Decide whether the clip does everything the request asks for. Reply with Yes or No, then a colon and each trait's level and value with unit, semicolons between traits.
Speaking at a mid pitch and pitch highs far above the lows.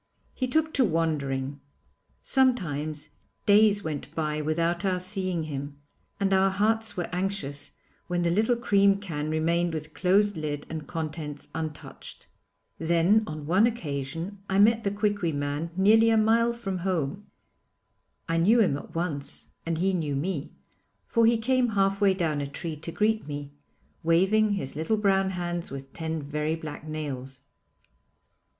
No: medium, 175 Hz; average, 5.0 semitones